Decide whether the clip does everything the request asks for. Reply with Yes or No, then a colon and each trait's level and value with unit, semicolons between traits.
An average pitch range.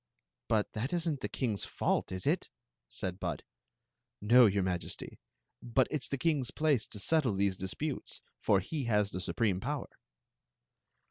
No: wide, 6.3 semitones